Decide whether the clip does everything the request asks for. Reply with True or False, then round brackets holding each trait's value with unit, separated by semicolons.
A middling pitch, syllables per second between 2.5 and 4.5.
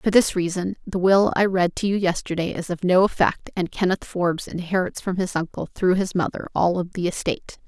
False (180 Hz; 5.5 syllables/s)